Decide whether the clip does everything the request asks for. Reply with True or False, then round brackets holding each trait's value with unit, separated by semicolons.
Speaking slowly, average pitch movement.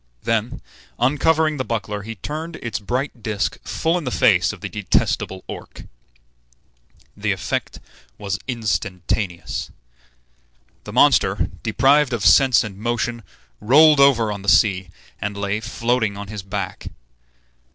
True (130 wpm; 4.3 semitones)